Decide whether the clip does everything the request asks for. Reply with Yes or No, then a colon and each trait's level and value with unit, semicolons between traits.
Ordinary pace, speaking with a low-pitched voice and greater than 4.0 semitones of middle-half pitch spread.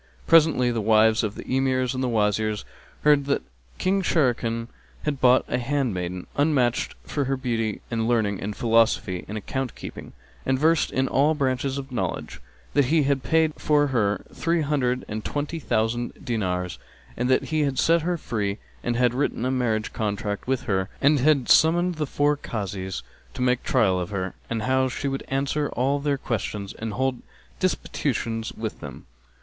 Yes: average, 170 wpm; low, 125 Hz; average, 4.5 semitones